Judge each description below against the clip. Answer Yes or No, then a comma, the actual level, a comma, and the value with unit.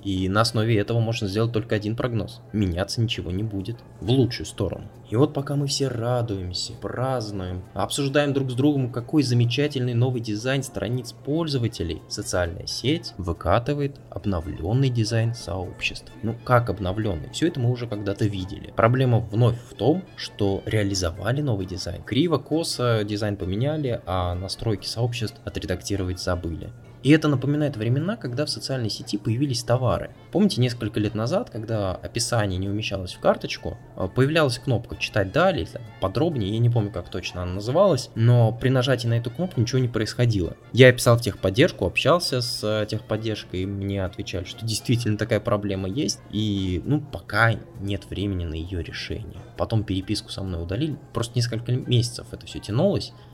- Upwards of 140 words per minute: Yes, fast, 160 wpm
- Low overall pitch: Yes, low, 115 Hz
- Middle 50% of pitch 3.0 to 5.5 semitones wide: Yes, average, 3.9 semitones